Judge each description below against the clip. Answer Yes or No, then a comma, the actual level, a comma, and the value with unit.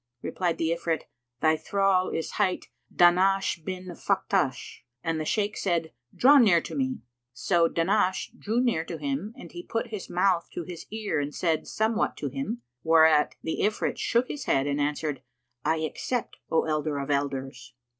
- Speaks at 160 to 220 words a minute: Yes, average, 170 wpm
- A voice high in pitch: No, medium, 170 Hz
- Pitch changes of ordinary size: Yes, average, 4.6 semitones